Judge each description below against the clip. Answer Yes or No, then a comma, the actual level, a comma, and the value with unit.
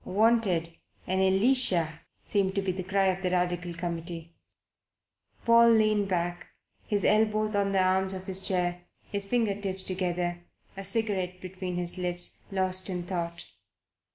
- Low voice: No, medium, 185 Hz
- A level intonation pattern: Yes, narrow, 2.2 semitones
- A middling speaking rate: Yes, average, 150 wpm